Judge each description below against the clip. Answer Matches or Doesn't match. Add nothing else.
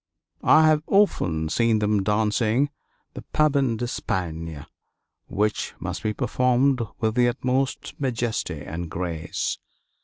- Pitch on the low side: Matches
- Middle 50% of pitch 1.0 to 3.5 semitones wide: Doesn't match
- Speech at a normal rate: Doesn't match